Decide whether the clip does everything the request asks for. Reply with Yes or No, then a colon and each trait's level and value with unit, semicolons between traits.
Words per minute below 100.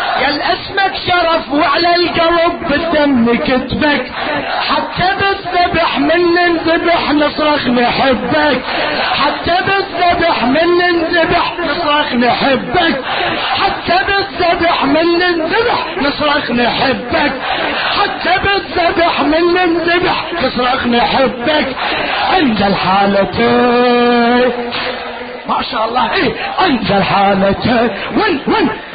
Yes: average, 85 wpm